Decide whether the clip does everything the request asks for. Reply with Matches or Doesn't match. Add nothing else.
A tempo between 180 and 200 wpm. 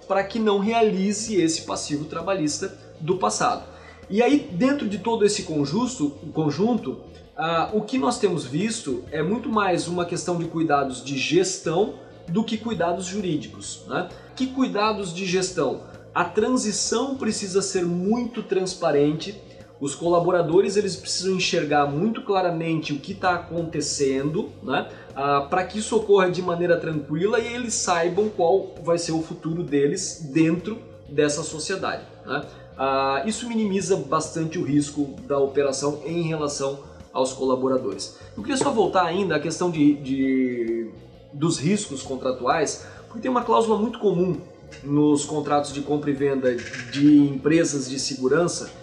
Doesn't match